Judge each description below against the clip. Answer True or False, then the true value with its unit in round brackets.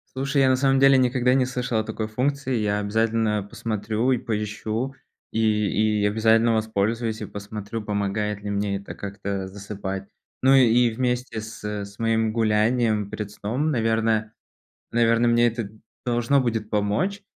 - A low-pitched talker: True (110 Hz)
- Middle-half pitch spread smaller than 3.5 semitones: True (2.5 semitones)